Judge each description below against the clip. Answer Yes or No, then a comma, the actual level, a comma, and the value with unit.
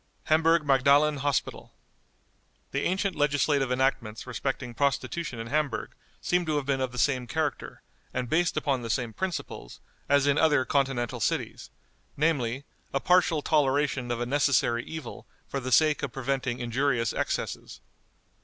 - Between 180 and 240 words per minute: No, average, 145 wpm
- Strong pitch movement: No, average, 3.2 semitones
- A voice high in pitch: No, medium, 140 Hz